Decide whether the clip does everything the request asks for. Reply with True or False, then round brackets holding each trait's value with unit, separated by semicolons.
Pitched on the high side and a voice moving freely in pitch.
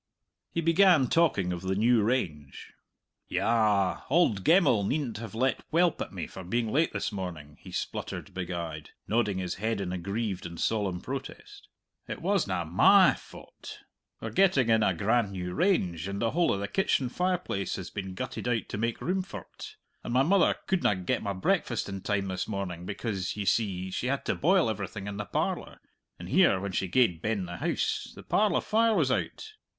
False (105 Hz; 6.3 semitones)